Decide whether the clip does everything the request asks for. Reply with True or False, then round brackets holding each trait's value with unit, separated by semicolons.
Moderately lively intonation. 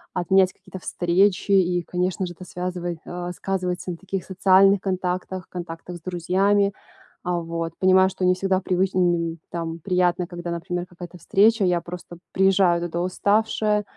False (1.5 semitones)